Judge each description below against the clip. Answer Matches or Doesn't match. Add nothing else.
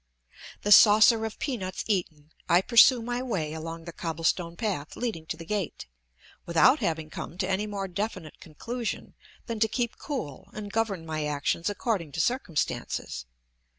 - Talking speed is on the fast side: Doesn't match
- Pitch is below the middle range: Doesn't match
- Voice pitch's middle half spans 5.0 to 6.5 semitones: Matches